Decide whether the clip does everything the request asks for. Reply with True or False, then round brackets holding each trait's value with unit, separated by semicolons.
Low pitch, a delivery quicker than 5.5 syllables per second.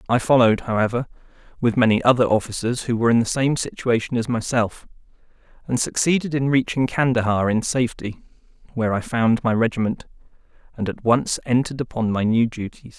True (120 Hz; 6.0 syllables/s)